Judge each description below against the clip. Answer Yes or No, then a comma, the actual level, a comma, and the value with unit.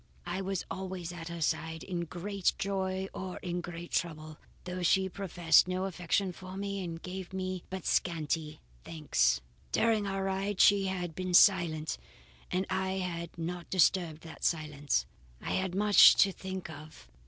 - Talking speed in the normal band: Yes, average, 160 wpm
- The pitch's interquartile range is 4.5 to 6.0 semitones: No, narrow, 2.4 semitones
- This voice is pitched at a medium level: Yes, medium, 180 Hz